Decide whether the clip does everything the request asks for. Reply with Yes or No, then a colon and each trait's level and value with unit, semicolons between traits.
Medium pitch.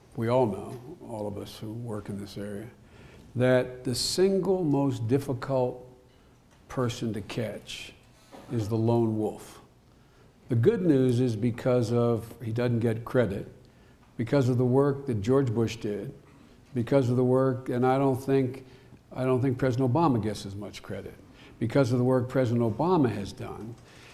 No: low, 125 Hz